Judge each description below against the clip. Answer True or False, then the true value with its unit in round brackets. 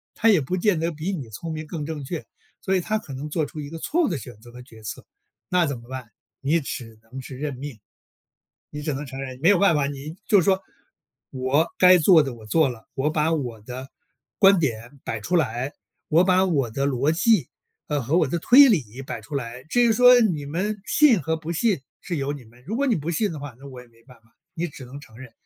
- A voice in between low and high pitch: True (150 Hz)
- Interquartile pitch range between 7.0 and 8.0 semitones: False (5.2 semitones)